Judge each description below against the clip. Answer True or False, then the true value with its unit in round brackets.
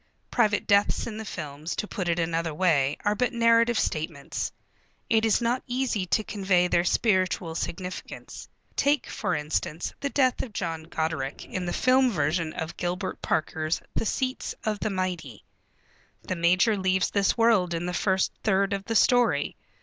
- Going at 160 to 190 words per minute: True (165 wpm)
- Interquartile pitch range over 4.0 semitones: True (5.0 semitones)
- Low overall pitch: False (185 Hz)